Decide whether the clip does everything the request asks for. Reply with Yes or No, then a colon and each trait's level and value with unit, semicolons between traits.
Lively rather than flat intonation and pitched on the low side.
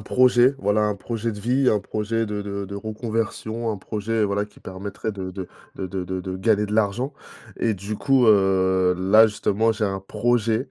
No: narrow, 2.5 semitones; low, 105 Hz